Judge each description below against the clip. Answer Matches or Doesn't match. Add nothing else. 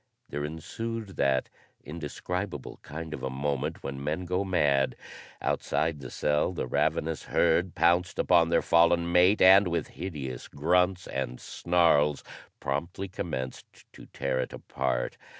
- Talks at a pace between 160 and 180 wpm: Doesn't match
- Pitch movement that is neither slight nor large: Matches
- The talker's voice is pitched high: Doesn't match